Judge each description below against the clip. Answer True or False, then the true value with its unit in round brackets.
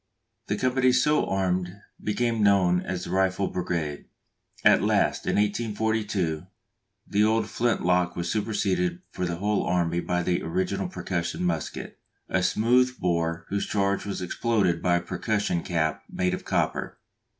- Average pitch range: True (3.6 semitones)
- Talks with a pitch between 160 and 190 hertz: False (95 Hz)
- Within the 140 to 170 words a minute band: True (150 wpm)